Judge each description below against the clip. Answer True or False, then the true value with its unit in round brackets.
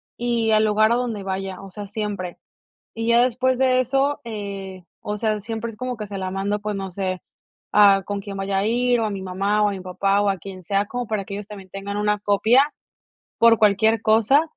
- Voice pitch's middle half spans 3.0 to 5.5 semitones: False (2.6 semitones)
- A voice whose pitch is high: True (210 Hz)